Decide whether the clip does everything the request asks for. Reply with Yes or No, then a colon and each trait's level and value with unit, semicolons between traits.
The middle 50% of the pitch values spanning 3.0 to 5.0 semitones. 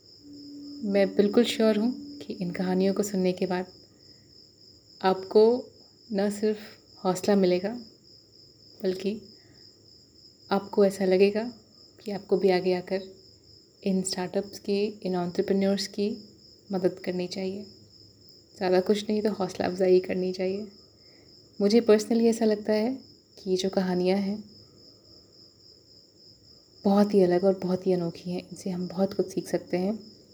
No: narrow, 2.4 semitones